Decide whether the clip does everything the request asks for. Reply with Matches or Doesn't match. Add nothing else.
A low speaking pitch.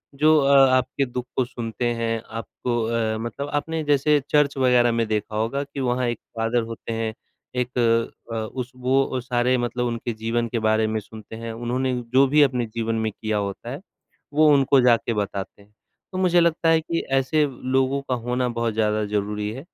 Matches